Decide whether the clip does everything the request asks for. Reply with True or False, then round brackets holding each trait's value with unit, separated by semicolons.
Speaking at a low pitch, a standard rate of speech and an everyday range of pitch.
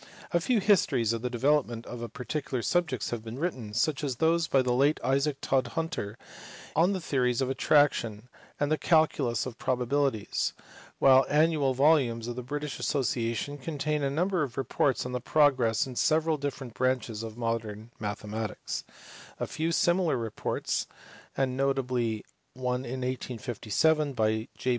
True (130 Hz; 160 wpm; 4.1 semitones)